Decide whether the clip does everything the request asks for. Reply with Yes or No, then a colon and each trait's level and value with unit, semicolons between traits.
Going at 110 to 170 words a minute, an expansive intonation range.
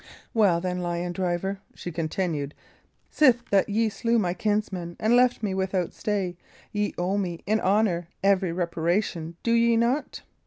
No: average, 155 wpm; average, 3.7 semitones